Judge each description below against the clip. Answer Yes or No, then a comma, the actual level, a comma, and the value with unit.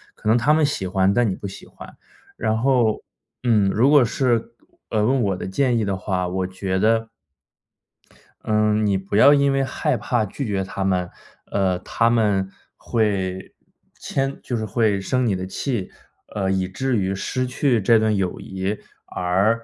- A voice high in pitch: No, low, 105 Hz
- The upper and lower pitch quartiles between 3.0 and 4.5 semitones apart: Yes, average, 4.0 semitones